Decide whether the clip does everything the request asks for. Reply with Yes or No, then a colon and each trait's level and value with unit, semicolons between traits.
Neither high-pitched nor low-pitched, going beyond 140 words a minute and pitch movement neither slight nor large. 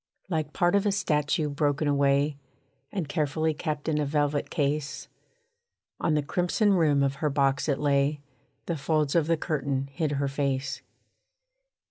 No: medium, 150 Hz; average, 155 wpm; narrow, 2.1 semitones